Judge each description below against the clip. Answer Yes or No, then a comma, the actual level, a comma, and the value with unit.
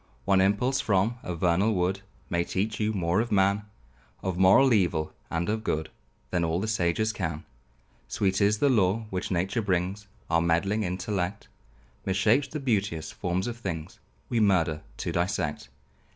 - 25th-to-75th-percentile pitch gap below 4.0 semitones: Yes, average, 3.5 semitones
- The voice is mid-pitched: No, very low, 95 Hz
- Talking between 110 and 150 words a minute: No, average, 160 wpm